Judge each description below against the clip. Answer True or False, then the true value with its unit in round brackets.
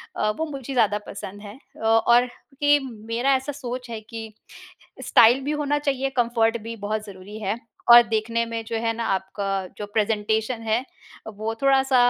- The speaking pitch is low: False (230 Hz)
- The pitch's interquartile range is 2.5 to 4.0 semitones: True (3.1 semitones)